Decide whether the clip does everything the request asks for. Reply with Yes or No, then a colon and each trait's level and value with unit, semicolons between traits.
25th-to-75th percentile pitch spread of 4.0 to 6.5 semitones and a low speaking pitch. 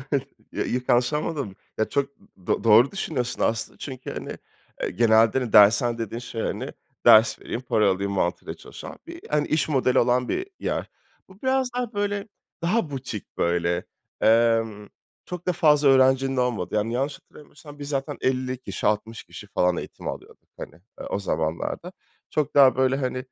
Yes: average, 4.7 semitones; low, 125 Hz